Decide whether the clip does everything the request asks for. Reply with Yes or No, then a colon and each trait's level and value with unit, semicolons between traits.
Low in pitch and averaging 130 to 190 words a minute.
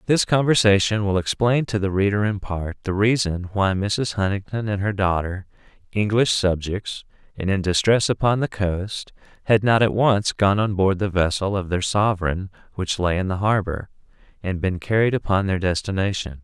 Yes: low, 100 Hz; average, 175 wpm